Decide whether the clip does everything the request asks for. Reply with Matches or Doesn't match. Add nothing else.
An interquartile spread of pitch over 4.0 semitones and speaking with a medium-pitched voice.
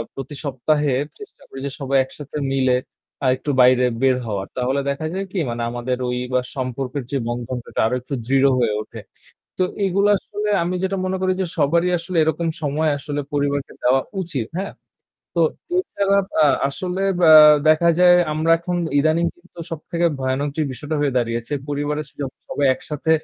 Matches